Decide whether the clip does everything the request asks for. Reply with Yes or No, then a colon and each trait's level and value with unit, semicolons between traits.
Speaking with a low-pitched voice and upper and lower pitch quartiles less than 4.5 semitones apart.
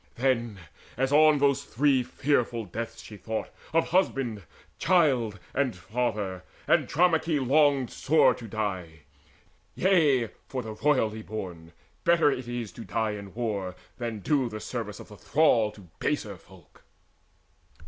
No: low, 120 Hz; average, 5.1 semitones